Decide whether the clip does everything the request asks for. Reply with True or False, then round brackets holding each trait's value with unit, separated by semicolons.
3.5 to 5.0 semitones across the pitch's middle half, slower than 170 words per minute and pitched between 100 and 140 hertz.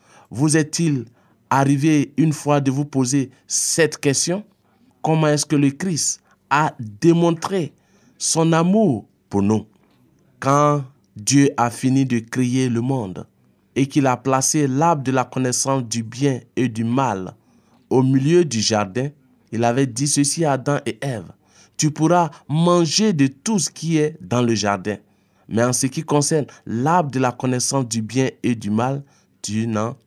True (4.3 semitones; 160 wpm; 135 Hz)